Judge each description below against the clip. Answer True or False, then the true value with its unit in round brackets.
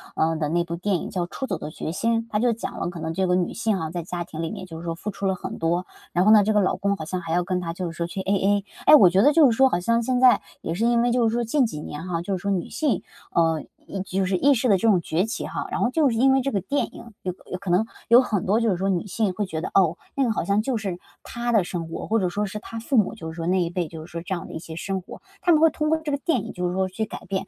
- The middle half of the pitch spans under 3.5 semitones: False (4.8 semitones)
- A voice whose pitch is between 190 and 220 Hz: True (195 Hz)